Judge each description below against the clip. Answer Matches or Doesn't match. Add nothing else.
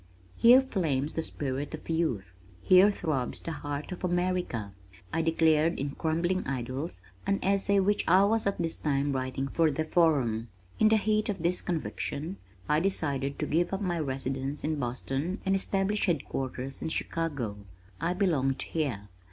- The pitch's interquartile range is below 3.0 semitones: Doesn't match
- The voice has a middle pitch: Matches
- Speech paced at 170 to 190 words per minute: Doesn't match